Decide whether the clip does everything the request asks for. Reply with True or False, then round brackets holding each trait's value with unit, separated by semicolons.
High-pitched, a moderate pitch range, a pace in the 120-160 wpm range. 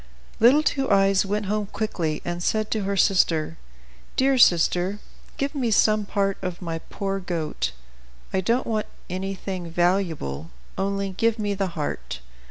True (195 Hz; 3.3 semitones; 150 wpm)